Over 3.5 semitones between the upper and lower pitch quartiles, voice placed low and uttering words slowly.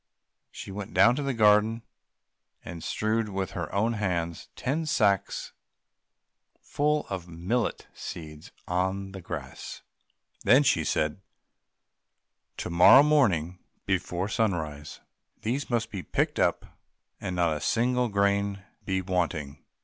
Yes: average, 4.8 semitones; low, 100 Hz; slow, 125 wpm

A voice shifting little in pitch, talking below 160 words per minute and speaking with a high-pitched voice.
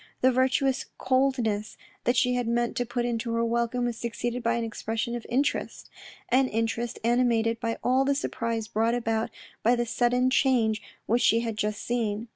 No: narrow, 1.6 semitones; average, 185 wpm; high, 235 Hz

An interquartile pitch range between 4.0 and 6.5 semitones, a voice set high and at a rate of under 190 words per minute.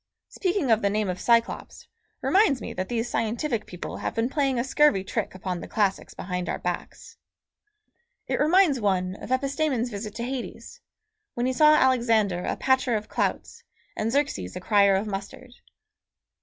Yes: average, 5.1 semitones; high, 230 Hz; average, 170 wpm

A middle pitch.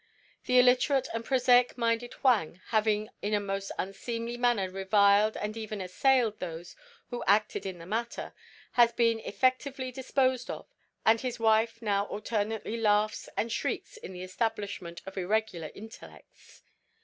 No: high, 220 Hz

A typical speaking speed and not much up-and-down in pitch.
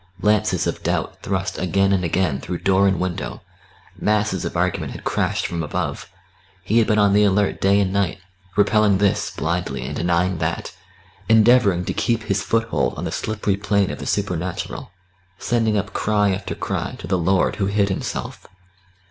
Yes: average, 175 wpm; narrow, 2.3 semitones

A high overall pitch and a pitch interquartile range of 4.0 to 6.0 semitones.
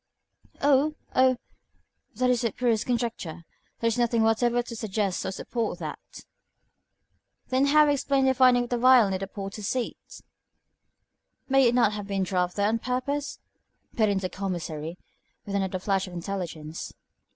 Yes: high, 225 Hz; average, 4.6 semitones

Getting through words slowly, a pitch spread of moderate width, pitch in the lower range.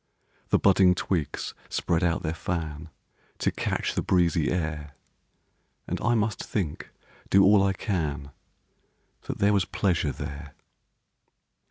Yes: slow, 130 wpm; average, 4.3 semitones; very low, 85 Hz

